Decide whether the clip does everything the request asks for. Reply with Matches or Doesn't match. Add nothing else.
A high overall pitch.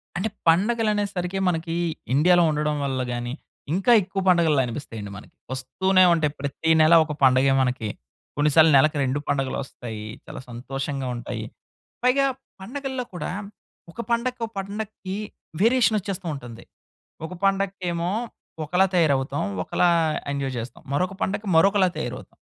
Doesn't match